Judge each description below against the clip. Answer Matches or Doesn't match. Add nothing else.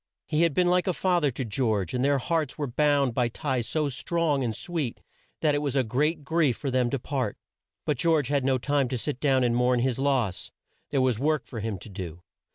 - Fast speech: Matches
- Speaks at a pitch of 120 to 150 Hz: Matches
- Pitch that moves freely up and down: Doesn't match